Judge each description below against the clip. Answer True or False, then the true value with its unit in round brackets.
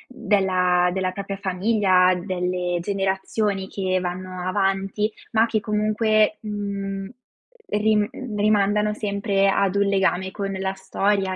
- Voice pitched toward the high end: True (195 Hz)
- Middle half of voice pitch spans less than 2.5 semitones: True (1.8 semitones)